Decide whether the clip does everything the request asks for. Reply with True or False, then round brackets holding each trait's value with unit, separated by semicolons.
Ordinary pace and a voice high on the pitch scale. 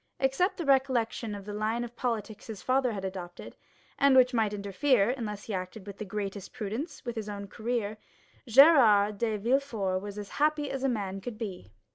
True (190 wpm; 220 Hz)